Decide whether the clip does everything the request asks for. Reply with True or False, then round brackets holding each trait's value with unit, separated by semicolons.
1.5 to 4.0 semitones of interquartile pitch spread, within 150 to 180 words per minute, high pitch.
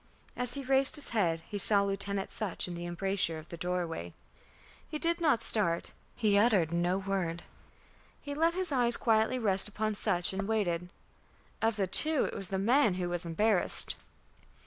False (4.8 semitones; 175 wpm; 200 Hz)